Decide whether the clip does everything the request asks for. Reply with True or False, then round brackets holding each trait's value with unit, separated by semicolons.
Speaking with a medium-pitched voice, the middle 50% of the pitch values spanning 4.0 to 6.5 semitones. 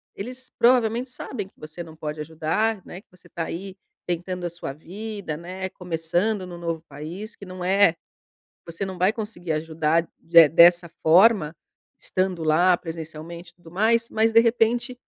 True (180 Hz; 4.3 semitones)